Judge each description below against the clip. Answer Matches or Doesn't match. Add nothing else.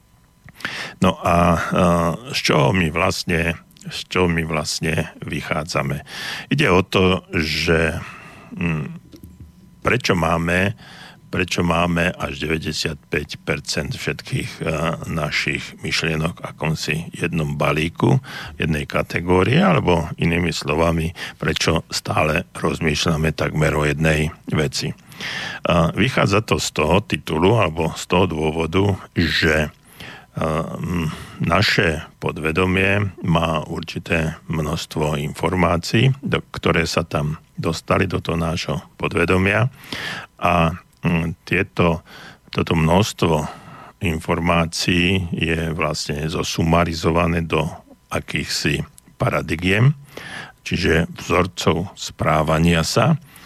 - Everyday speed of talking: Doesn't match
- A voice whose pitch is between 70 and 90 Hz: Matches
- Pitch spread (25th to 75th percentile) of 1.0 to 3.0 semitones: Matches